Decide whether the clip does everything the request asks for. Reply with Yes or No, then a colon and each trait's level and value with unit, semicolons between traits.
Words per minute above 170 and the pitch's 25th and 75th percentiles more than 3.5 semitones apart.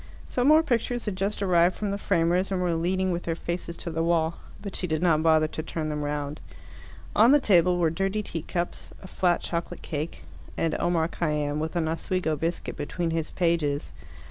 No: average, 195 wpm; narrow, 2.6 semitones